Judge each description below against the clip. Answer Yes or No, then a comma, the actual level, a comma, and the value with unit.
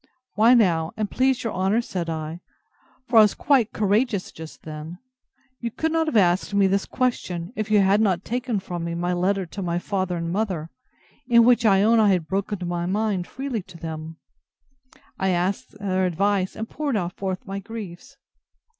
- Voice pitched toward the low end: No, high, 195 Hz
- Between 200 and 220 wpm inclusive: No, average, 185 wpm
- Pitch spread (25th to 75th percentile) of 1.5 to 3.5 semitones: No, average, 4.0 semitones